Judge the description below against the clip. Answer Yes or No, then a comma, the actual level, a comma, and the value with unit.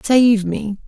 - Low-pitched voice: No, high, 215 Hz